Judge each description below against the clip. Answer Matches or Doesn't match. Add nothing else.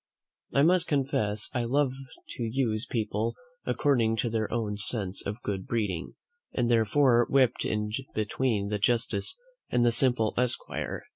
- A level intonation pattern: Doesn't match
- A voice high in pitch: Doesn't match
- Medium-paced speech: Matches